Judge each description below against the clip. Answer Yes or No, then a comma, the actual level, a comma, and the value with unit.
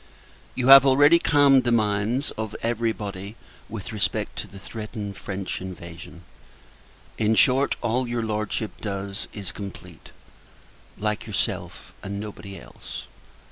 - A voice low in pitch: Yes, low, 110 Hz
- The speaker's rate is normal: No, slow, 130 wpm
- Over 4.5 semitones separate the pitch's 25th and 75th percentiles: No, average, 3.2 semitones